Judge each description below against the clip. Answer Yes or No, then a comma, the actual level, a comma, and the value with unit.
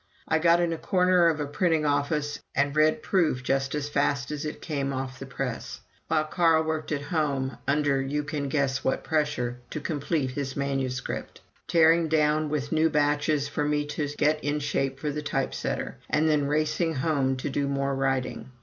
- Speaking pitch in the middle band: Yes, medium, 145 Hz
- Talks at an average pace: Yes, average, 190 wpm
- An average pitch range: No, narrow, 2.2 semitones